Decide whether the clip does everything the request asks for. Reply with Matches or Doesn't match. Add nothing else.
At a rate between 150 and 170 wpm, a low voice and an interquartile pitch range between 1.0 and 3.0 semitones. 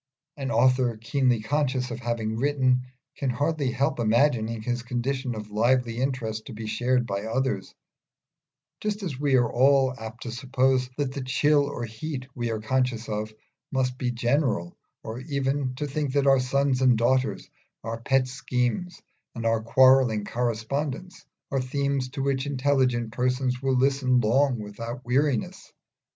Matches